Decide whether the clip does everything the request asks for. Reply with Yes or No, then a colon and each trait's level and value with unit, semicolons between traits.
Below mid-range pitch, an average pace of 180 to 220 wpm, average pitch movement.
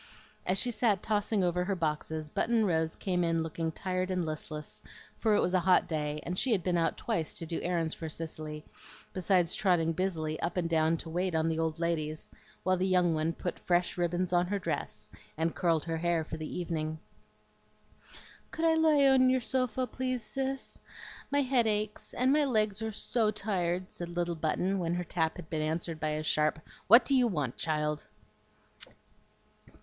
No: medium, 175 Hz; average, 190 wpm; average, 4.4 semitones